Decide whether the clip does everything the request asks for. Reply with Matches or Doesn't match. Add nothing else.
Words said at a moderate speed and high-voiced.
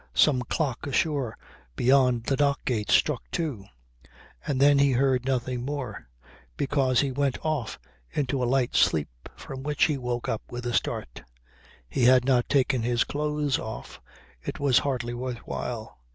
Doesn't match